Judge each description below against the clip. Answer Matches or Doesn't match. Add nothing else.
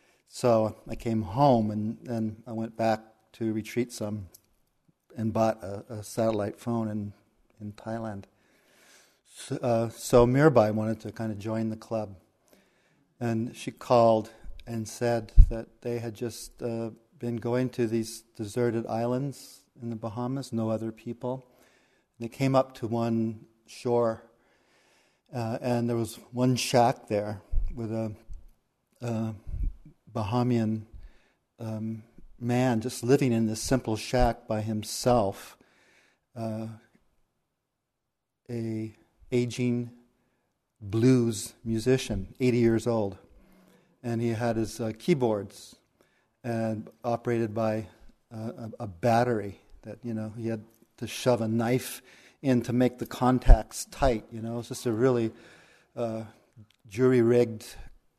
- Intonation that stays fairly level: Matches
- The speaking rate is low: Matches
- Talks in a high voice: Doesn't match